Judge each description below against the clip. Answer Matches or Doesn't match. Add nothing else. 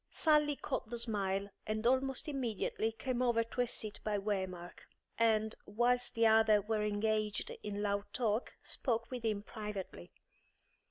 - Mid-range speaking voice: Doesn't match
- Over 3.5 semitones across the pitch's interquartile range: Doesn't match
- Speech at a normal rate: Matches